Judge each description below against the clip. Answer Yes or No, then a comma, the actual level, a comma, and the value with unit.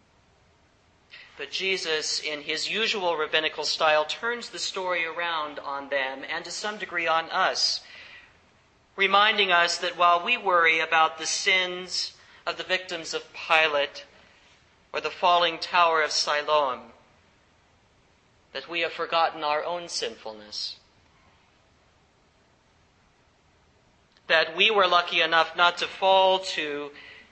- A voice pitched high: No, medium, 160 Hz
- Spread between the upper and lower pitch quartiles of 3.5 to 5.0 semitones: Yes, average, 4.1 semitones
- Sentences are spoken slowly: Yes, slow, 120 wpm